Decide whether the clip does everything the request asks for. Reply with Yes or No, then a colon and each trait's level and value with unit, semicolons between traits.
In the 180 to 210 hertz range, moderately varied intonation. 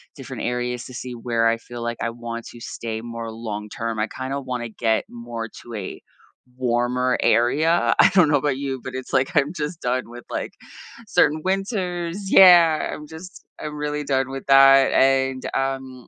No: low, 130 Hz; average, 4.0 semitones